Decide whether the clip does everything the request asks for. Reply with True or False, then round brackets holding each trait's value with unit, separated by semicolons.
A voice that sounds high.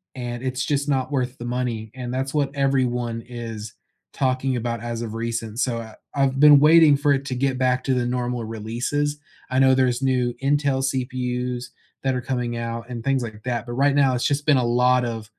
False (125 Hz)